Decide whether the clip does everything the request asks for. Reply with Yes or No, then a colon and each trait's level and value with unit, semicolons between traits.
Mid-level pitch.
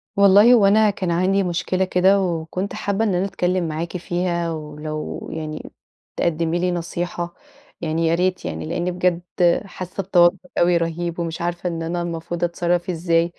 Yes: medium, 175 Hz